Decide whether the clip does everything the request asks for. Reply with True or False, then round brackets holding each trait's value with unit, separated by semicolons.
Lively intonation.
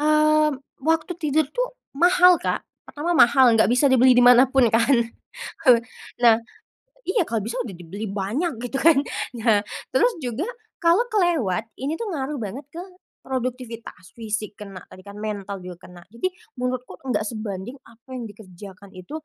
True (6.2 semitones)